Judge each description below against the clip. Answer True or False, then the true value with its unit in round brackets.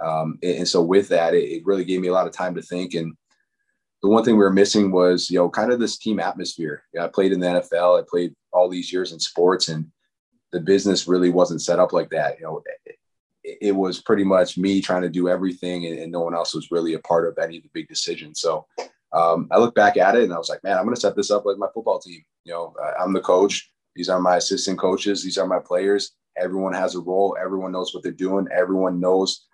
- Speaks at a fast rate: True (265 wpm)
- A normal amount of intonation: False (1.7 semitones)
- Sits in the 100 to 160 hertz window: False (90 Hz)